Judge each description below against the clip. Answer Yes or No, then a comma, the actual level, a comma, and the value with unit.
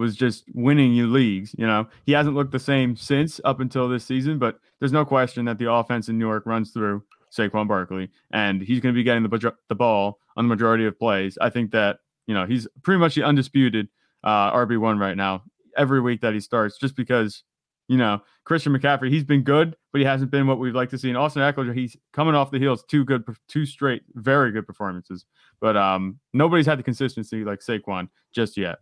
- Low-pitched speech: Yes, low, 120 Hz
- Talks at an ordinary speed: No, fast, 225 wpm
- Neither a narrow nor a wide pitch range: Yes, average, 4.0 semitones